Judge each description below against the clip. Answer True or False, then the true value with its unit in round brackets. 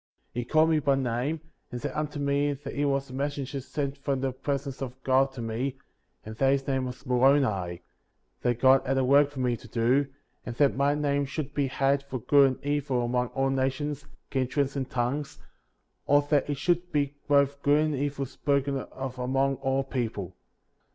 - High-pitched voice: False (135 Hz)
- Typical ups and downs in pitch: False (1.7 semitones)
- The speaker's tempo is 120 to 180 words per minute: False (200 wpm)